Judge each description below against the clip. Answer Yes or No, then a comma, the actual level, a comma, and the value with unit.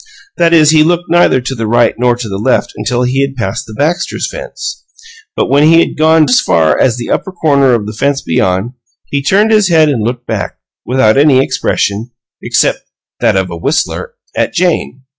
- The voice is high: No, low, 135 Hz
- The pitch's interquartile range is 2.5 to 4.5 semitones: No, wide, 5.5 semitones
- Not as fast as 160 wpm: No, average, 200 wpm